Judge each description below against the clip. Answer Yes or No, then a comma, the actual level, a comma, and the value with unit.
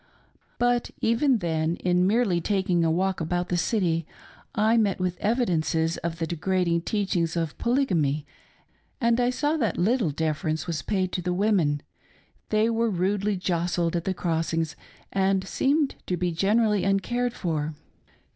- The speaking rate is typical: Yes, average, 155 wpm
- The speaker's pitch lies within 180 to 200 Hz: Yes, medium, 185 Hz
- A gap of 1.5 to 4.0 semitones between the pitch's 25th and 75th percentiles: No, average, 4.4 semitones